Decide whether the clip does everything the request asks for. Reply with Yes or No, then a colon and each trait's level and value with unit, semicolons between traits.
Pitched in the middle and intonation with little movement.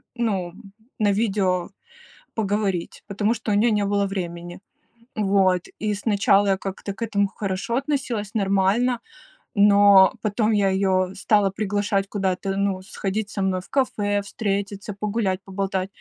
No: high, 200 Hz; narrow, 1.6 semitones